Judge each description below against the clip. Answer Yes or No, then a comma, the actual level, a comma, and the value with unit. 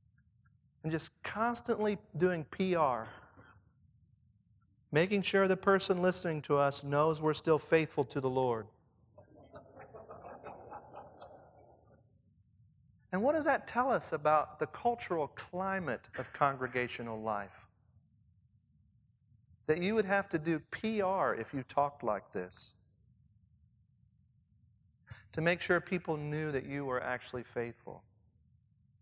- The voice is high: No, low, 135 Hz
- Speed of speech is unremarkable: No, slow, 110 wpm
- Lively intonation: Yes, wide, 6.5 semitones